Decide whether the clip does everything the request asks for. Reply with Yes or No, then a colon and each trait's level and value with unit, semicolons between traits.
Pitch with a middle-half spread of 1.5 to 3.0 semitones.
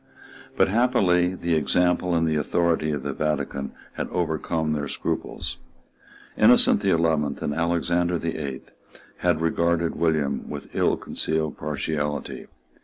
Yes: narrow, 2.4 semitones